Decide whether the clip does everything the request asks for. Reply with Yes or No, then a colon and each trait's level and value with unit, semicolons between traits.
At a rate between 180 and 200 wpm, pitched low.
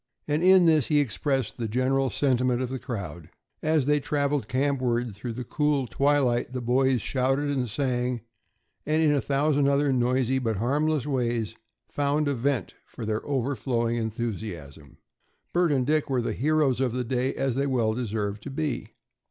No: average, 170 wpm; low, 130 Hz